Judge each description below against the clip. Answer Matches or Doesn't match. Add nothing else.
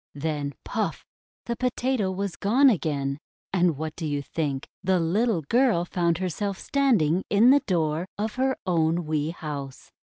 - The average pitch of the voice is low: Doesn't match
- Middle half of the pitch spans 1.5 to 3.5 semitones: Doesn't match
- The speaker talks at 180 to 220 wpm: Doesn't match